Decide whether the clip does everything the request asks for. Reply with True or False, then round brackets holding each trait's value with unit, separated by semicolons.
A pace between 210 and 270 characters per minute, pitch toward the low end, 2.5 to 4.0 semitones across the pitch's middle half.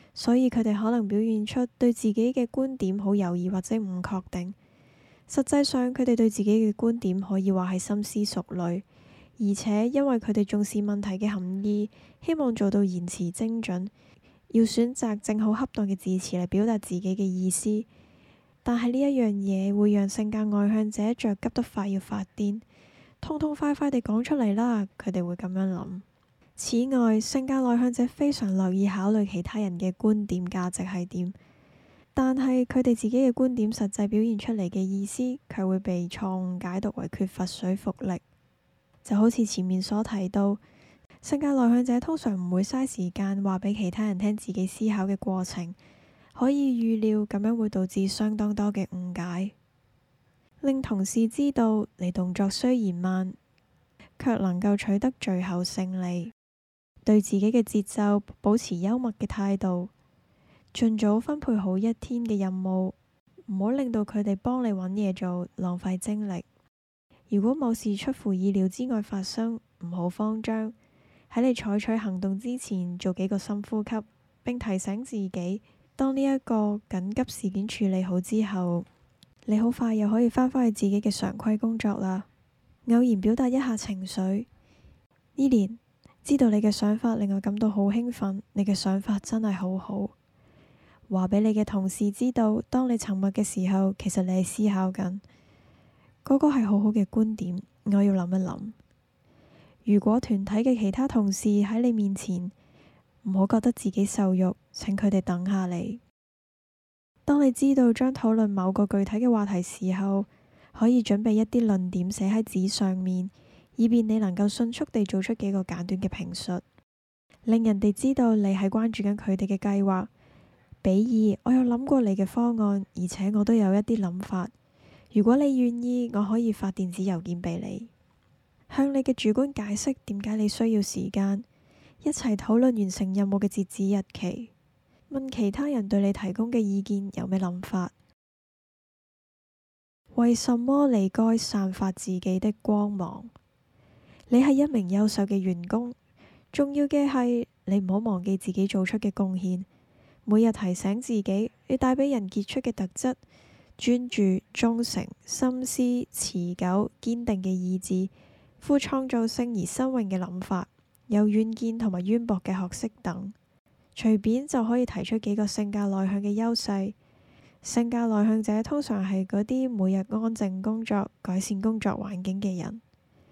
False (240 characters per minute; 210 Hz; 3.3 semitones)